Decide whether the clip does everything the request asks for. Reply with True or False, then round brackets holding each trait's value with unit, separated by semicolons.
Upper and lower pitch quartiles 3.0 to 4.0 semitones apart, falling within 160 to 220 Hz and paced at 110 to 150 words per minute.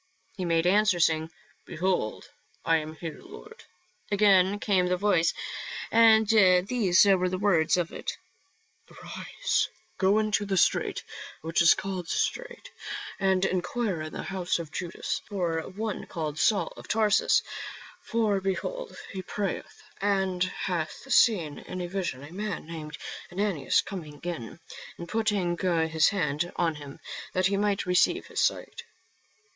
True (3.6 semitones; 185 Hz; 145 wpm)